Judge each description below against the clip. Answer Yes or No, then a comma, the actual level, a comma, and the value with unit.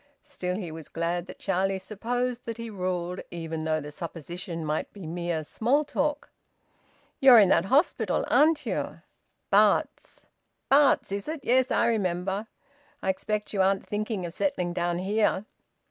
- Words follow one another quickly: No, average, 155 wpm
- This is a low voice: No, high, 195 Hz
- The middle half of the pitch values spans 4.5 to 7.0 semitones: Yes, average, 5.2 semitones